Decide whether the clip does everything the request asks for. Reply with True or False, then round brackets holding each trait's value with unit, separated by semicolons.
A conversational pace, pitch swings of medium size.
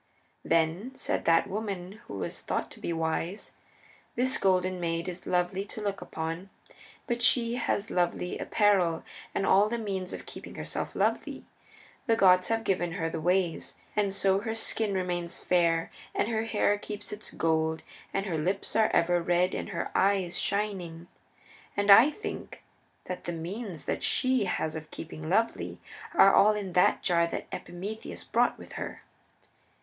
True (165 wpm; 3.5 semitones)